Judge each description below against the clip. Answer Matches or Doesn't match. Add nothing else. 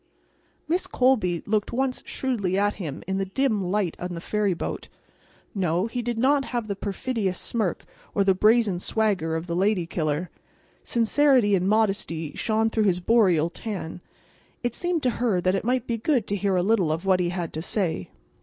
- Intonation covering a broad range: Doesn't match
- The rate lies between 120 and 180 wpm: Doesn't match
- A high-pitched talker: Matches